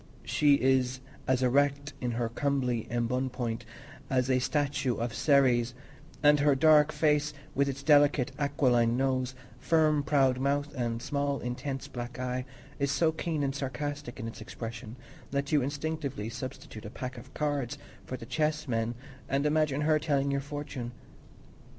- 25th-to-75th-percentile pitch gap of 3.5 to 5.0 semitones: No, average, 2.8 semitones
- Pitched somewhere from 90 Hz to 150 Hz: Yes, low, 135 Hz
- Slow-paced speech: No, average, 155 wpm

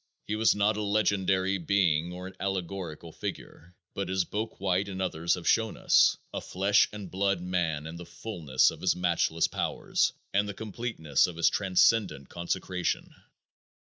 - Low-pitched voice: Yes, very low, 95 Hz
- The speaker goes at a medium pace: Yes, average, 165 wpm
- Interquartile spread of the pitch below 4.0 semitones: Yes, average, 2.8 semitones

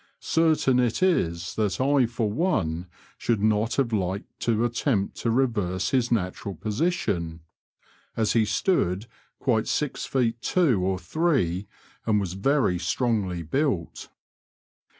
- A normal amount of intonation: No, wide, 5.9 semitones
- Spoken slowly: Yes, slow, 130 wpm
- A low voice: Yes, low, 110 Hz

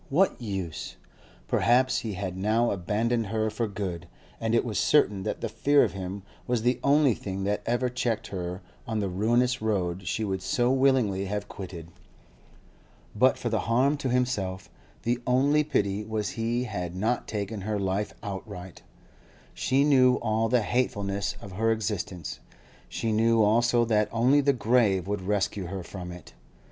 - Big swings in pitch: No, average, 3.9 semitones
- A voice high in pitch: No, low, 110 Hz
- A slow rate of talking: No, average, 165 wpm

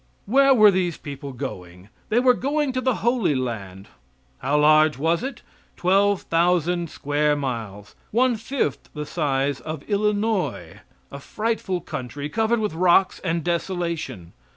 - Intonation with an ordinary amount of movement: No, wide, 7.0 semitones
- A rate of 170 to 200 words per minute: No, average, 140 wpm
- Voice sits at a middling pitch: Yes, medium, 170 Hz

